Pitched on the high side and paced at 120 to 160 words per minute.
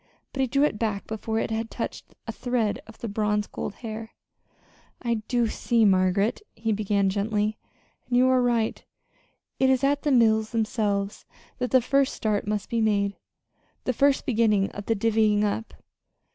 No: high, 220 Hz; average, 170 wpm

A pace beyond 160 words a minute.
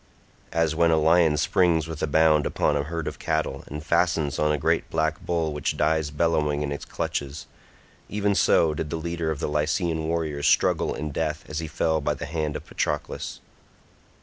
Yes: average, 190 wpm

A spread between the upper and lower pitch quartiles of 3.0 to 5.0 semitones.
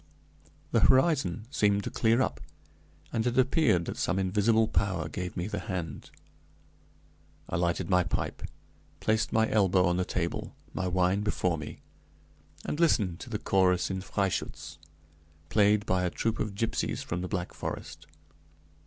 Yes: average, 3.4 semitones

